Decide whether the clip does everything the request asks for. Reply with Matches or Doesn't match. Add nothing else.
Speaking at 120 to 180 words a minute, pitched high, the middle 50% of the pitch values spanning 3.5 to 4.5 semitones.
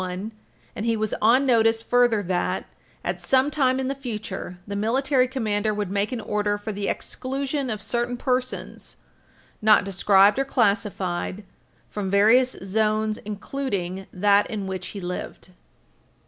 Matches